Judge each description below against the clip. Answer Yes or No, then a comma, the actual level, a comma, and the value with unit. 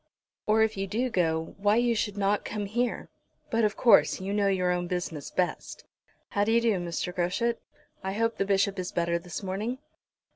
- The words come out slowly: No, average, 190 wpm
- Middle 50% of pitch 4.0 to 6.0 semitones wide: No, average, 3.6 semitones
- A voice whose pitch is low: No, high, 200 Hz